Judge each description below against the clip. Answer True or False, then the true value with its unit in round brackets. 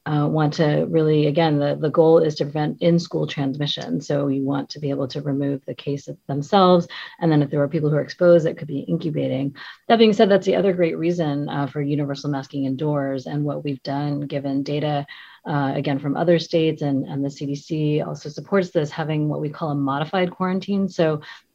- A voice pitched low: False (150 Hz)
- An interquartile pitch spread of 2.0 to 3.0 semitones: True (2.6 semitones)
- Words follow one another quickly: True (215 wpm)